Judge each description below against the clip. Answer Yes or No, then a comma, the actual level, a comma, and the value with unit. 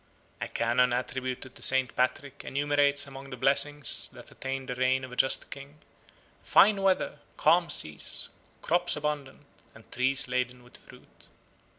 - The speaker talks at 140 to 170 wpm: Yes, average, 150 wpm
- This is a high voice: No, low, 135 Hz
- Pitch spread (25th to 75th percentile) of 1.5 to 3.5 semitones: Yes, narrow, 2.4 semitones